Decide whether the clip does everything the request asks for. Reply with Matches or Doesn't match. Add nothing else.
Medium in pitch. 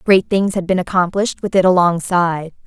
Matches